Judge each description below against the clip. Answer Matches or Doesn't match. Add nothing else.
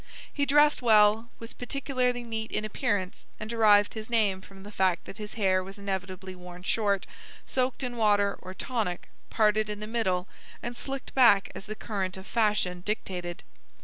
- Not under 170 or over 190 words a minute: Matches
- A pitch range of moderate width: Matches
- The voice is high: Matches